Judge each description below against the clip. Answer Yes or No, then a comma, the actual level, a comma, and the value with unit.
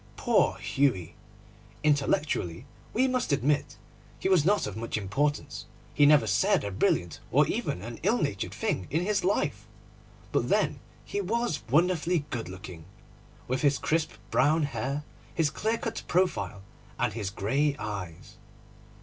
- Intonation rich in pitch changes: Yes, wide, 8.2 semitones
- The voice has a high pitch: No, medium, 145 Hz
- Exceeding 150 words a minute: No, average, 145 wpm